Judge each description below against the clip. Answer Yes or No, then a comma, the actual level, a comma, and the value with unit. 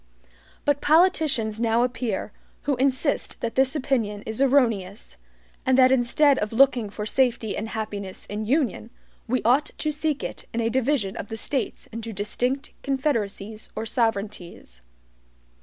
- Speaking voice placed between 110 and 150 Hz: No, high, 235 Hz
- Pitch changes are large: No, average, 4.1 semitones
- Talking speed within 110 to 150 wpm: Yes, average, 145 wpm